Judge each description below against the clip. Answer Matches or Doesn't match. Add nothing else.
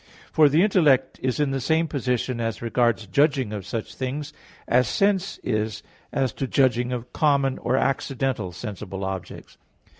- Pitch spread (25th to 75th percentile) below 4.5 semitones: Matches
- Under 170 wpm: Matches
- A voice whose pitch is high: Doesn't match